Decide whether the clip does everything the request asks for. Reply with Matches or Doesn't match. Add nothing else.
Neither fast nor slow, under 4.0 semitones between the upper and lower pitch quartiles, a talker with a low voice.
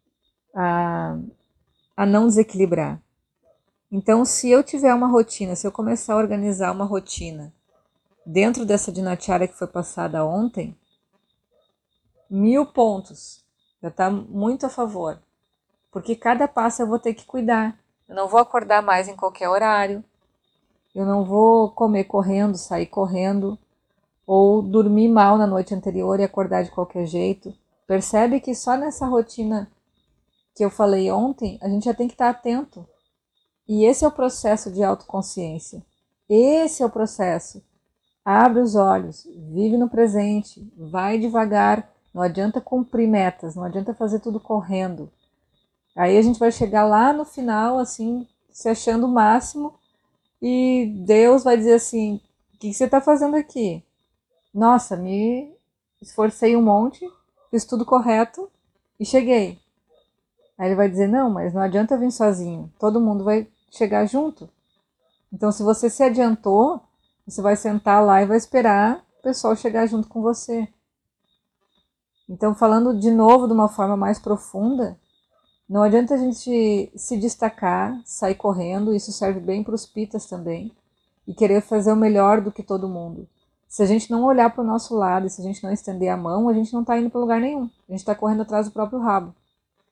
Doesn't match